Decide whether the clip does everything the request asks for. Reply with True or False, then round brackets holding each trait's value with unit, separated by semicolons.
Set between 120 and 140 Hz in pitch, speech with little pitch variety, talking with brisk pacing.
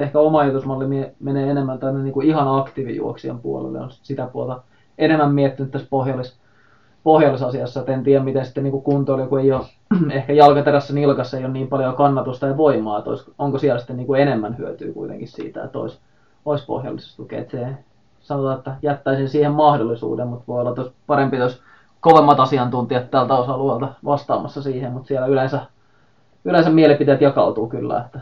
True (135 Hz; 2.1 semitones; 160 wpm)